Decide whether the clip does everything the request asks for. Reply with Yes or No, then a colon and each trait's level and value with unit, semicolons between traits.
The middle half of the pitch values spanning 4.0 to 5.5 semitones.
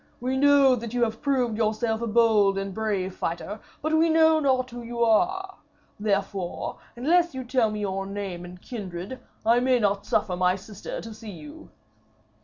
Yes: average, 4.6 semitones